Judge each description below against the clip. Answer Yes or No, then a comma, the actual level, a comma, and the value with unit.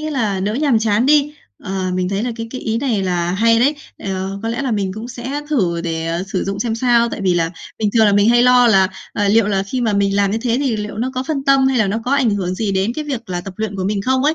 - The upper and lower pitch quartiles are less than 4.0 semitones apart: No, average, 4.3 semitones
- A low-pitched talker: No, high, 220 Hz